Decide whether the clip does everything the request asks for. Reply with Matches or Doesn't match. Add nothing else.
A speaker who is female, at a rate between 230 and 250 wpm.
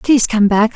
Matches